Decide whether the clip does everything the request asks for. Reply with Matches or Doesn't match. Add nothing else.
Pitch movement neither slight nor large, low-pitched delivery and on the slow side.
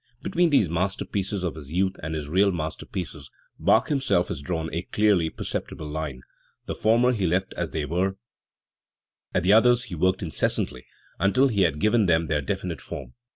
Doesn't match